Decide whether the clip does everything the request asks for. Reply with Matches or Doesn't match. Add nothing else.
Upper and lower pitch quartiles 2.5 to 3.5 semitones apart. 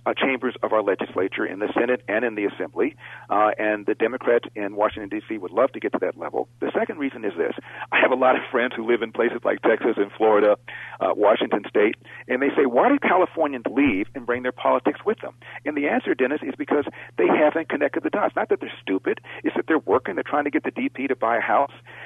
Doesn't match